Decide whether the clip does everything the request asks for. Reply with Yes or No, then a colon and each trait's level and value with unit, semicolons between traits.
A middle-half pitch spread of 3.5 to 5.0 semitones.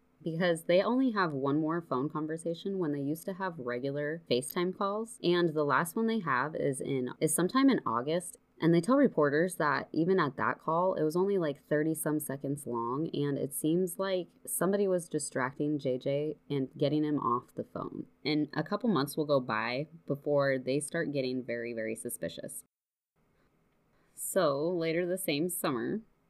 Yes: average, 4.2 semitones